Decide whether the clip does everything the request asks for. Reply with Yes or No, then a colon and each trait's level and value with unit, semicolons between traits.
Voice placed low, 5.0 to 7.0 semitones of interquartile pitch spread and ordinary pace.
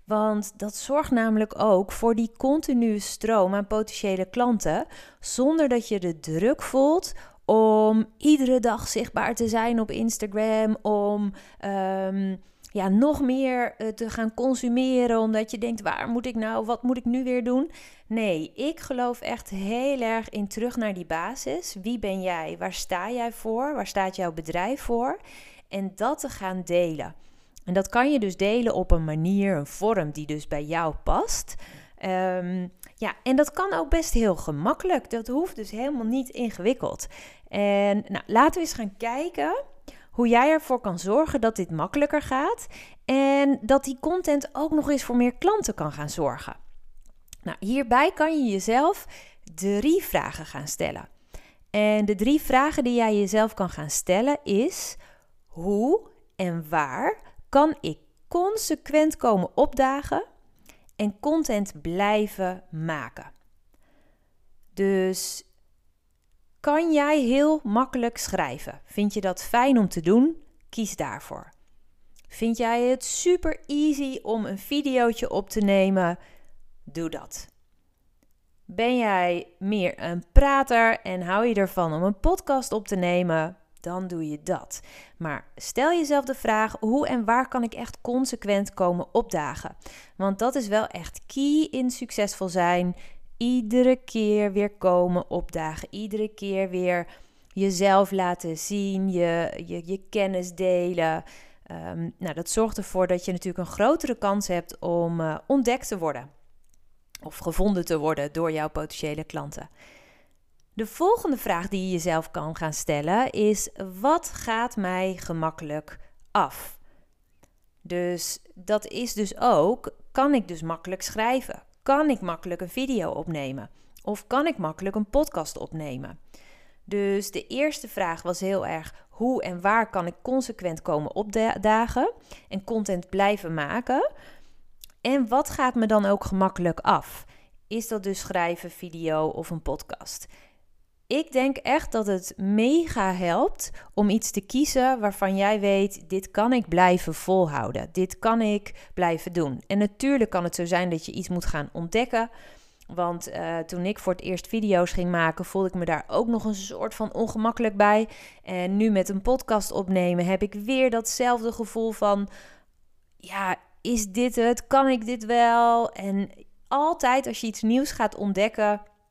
No: high, 210 Hz; wide, 5.5 semitones; average, 155 wpm